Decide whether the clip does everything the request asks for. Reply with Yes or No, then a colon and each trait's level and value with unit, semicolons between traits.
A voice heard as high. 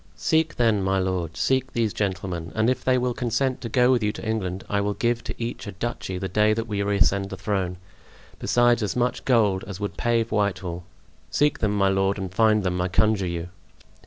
No: low, 105 Hz